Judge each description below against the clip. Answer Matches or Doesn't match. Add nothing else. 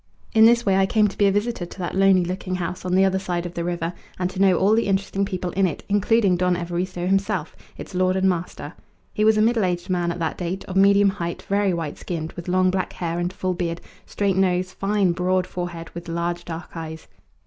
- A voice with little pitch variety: Matches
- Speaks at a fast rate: Matches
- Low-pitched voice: Doesn't match